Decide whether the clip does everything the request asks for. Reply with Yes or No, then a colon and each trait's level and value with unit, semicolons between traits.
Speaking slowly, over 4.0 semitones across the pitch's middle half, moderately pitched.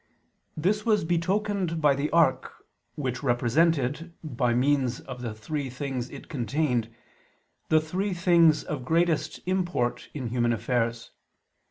Yes: slow, 130 wpm; wide, 5.4 semitones; medium, 150 Hz